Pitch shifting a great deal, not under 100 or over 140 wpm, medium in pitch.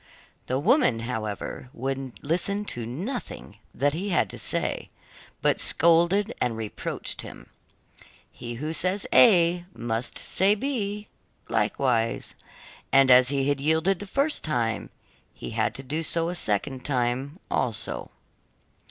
Yes: wide, 7.0 semitones; slow, 135 wpm; medium, 145 Hz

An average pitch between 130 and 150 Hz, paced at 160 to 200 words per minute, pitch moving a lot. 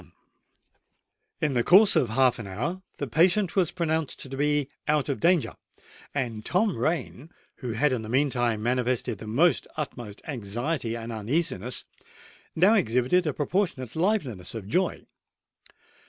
No: low, 135 Hz; average, 140 wpm; wide, 5.9 semitones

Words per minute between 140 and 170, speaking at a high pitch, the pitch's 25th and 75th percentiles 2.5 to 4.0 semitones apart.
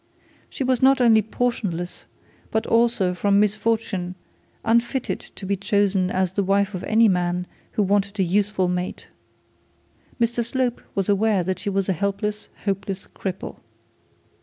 Yes: average, 145 wpm; high, 200 Hz; average, 3.0 semitones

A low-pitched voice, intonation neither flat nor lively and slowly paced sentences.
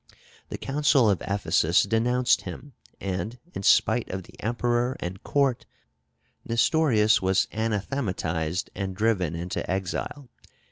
Yes: low, 105 Hz; average, 4.6 semitones; slow, 120 wpm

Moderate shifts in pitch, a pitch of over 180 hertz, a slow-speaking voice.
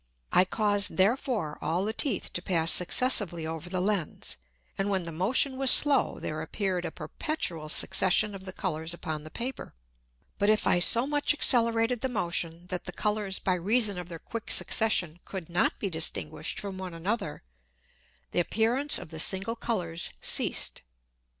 No: average, 4.9 semitones; high, 190 Hz; average, 170 wpm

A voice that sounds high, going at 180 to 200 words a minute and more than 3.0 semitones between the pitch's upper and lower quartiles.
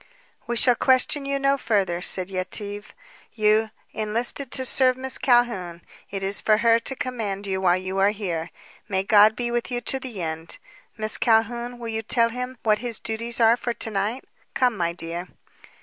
Yes: high, 220 Hz; average, 185 wpm; average, 3.8 semitones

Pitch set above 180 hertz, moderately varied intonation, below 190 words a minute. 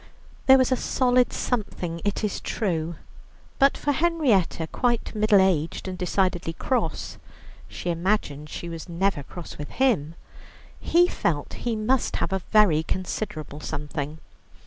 No: high, 190 Hz; wide, 6.6 semitones; average, 140 wpm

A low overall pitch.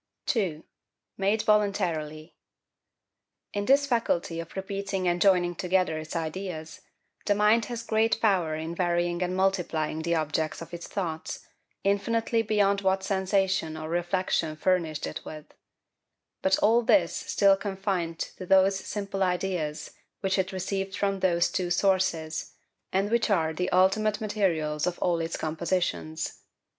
No: medium, 185 Hz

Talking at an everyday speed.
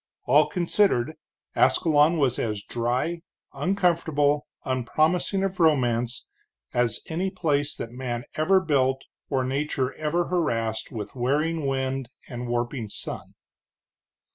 No: slow, 115 wpm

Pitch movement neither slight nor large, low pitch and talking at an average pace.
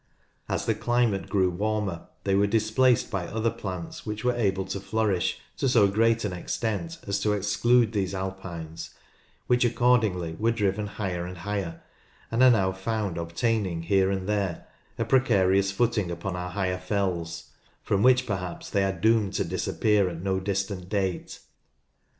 Yes: average, 3.1 semitones; low, 100 Hz; average, 160 wpm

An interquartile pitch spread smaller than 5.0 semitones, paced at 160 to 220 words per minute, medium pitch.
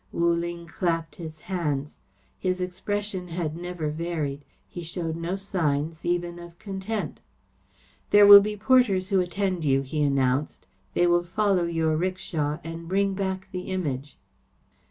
No: average, 2.9 semitones; average, 145 wpm; medium, 175 Hz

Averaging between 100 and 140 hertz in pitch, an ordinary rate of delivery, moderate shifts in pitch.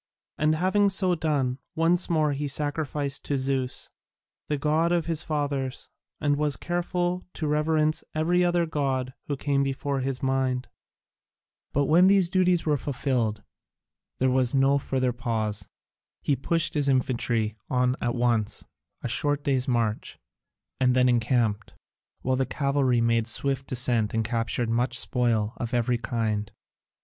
Yes: low, 135 Hz; average, 150 wpm; average, 3.8 semitones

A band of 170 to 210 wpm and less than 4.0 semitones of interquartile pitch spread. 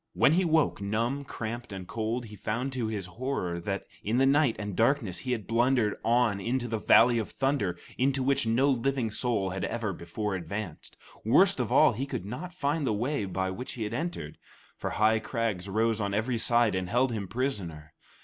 No: average, 200 wpm; average, 4.4 semitones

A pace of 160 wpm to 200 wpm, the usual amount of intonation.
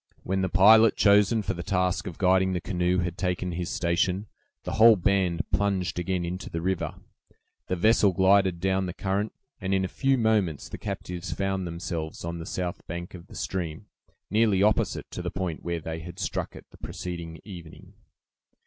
No: average, 185 wpm; narrow, 2.2 semitones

